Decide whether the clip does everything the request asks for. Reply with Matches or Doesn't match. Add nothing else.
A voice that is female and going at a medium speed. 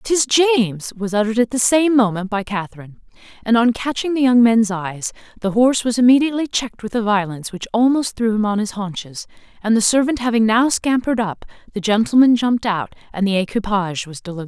Doesn't match